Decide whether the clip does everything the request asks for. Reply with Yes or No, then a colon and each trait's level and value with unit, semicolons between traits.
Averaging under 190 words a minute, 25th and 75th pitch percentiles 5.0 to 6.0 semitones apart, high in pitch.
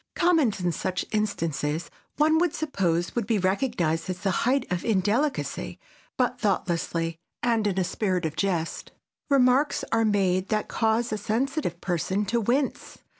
Yes: average, 150 wpm; wide, 5.6 semitones; high, 205 Hz